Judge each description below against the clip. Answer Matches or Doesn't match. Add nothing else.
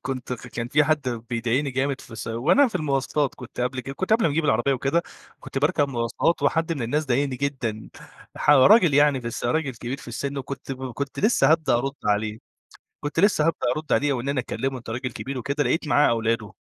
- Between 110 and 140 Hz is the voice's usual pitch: Matches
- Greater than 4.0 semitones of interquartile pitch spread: Doesn't match